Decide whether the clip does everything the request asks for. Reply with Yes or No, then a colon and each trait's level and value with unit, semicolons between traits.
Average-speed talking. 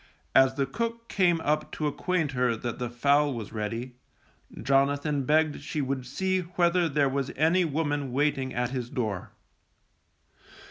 Yes: average, 150 wpm